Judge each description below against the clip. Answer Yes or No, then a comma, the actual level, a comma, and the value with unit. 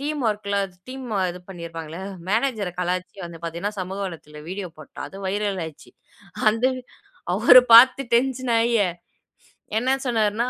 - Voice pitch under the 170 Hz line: No, high, 205 Hz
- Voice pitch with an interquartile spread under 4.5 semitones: No, average, 4.9 semitones